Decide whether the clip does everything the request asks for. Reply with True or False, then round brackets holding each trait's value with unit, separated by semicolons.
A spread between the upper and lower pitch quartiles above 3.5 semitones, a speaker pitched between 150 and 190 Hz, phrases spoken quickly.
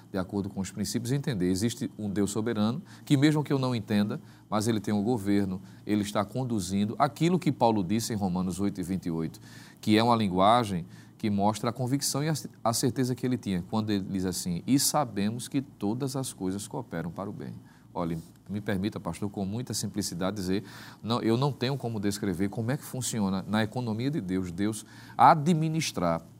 False (4.4 semitones; 110 Hz; 195 wpm)